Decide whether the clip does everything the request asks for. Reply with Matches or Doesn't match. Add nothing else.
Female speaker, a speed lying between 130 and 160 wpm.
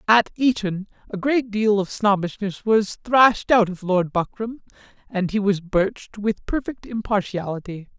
Doesn't match